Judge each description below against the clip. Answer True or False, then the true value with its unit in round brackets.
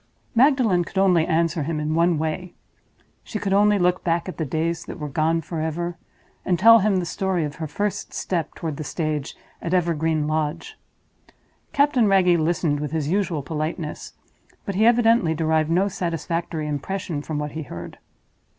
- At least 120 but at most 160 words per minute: False (170 wpm)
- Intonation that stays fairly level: False (3.4 semitones)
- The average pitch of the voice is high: False (165 Hz)